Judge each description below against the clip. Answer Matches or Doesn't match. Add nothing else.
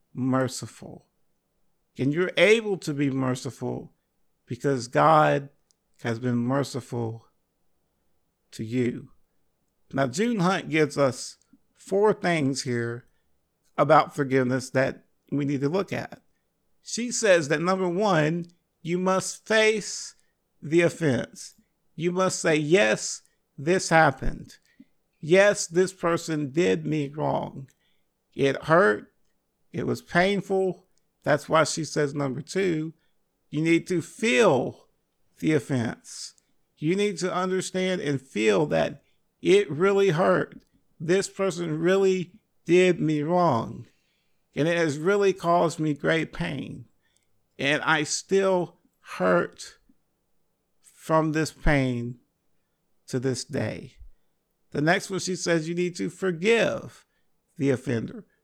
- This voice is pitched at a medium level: Matches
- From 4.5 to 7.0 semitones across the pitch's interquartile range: Matches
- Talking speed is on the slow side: Matches